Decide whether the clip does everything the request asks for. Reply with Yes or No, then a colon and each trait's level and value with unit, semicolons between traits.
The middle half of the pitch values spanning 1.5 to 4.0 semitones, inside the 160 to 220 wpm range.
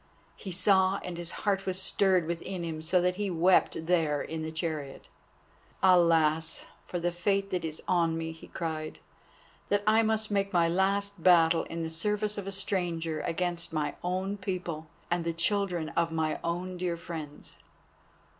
Yes: average, 2.7 semitones; average, 170 wpm